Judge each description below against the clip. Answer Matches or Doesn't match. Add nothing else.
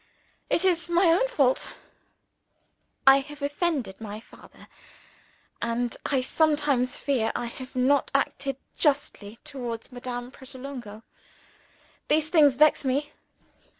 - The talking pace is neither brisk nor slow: Doesn't match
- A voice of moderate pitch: Doesn't match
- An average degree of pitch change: Matches